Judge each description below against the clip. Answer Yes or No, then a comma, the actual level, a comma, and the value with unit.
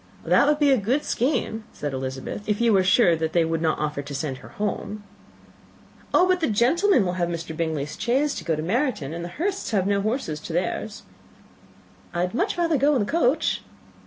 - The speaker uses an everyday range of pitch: No, wide, 8.5 semitones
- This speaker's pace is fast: Yes, fast, 215 wpm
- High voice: Yes, high, 205 Hz